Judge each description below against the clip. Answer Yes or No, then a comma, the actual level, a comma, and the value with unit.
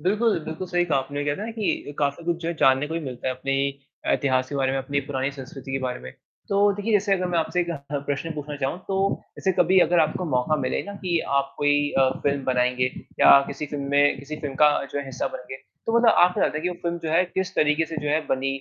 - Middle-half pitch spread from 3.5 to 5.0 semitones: Yes, average, 4.4 semitones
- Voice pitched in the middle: Yes, medium, 145 Hz